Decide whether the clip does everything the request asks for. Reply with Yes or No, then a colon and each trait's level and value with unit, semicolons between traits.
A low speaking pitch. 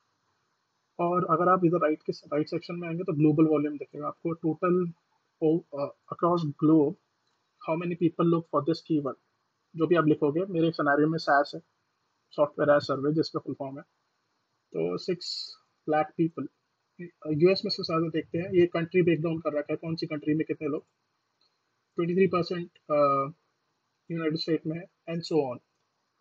No: medium, 160 Hz